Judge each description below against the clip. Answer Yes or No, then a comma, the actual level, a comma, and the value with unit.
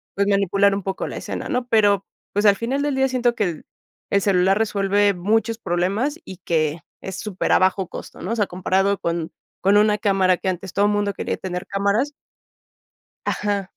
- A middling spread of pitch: No, narrow, 2.1 semitones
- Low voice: No, high, 200 Hz